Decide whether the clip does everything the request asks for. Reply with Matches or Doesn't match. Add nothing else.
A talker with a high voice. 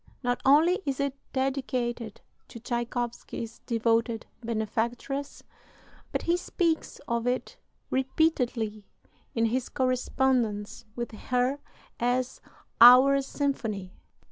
Matches